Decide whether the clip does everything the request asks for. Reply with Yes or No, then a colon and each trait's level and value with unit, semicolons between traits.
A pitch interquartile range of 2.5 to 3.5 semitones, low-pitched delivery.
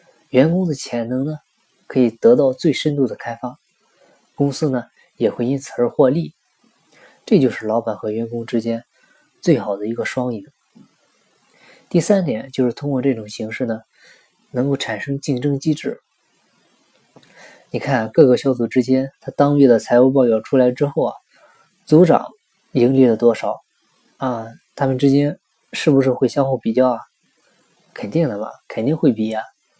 Yes: average, 3.2 semitones; low, 130 Hz